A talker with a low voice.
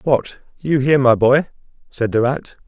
Yes: low, 130 Hz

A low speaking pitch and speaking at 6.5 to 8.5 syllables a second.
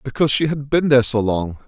Yes: low, 130 Hz; 6.6 syllables/s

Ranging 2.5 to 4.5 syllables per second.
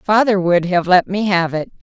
No: 4.7 syllables/s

